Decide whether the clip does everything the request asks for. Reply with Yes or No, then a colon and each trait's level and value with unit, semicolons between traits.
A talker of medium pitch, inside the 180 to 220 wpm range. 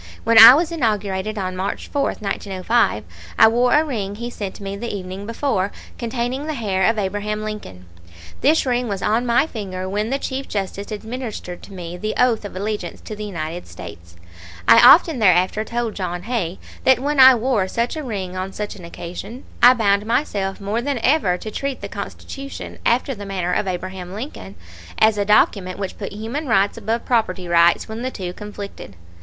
No: high, 210 Hz; average, 190 wpm